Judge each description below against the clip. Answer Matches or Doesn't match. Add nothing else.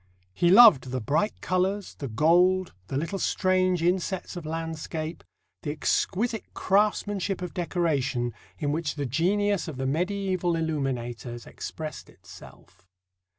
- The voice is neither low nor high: Matches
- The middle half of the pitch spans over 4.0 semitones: Matches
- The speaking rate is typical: Doesn't match